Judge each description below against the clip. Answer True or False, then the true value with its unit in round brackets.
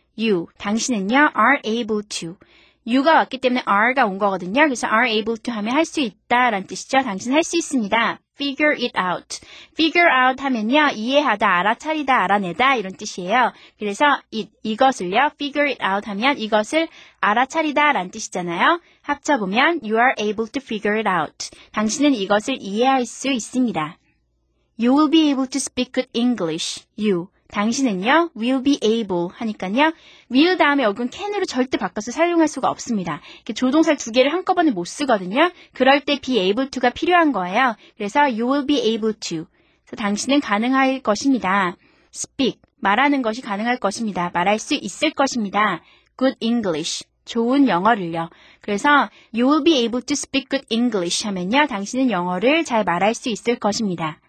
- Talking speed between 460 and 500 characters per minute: True (470 characters per minute)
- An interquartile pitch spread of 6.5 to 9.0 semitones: False (5.3 semitones)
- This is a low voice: False (245 Hz)